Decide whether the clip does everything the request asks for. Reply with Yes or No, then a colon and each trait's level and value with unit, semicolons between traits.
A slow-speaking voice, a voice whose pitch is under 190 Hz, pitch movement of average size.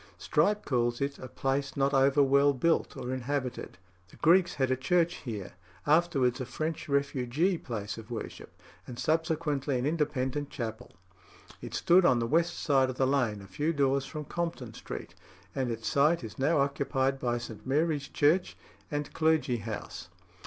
No: average, 165 wpm; medium, 140 Hz; average, 3.7 semitones